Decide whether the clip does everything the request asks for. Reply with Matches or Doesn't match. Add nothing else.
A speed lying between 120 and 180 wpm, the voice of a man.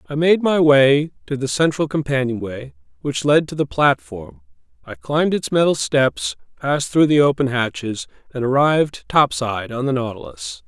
Matches